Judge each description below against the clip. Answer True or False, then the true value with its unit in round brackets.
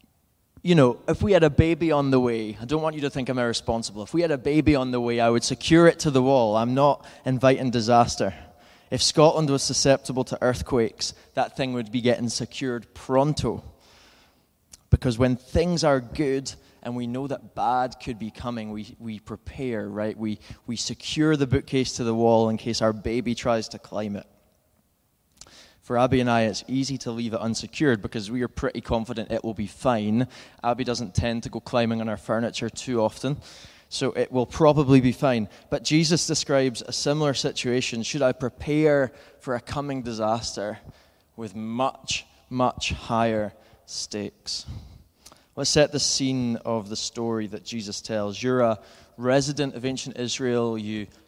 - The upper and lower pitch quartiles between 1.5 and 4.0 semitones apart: True (3.0 semitones)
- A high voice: False (120 Hz)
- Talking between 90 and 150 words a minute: False (180 wpm)